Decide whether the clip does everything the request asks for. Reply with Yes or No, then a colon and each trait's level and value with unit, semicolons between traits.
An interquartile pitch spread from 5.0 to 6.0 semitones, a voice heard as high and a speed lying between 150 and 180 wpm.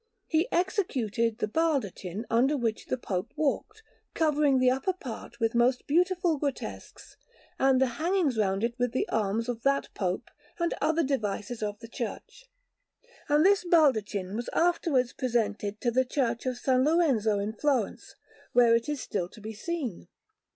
Yes: wide, 5.5 semitones; very high, 250 Hz; average, 160 wpm